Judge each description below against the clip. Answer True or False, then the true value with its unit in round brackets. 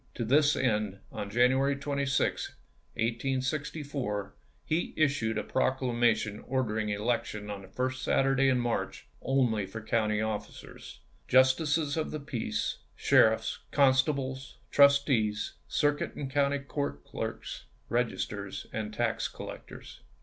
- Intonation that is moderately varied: True (4.2 semitones)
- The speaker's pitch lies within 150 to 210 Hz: False (130 Hz)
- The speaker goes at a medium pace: False (120 wpm)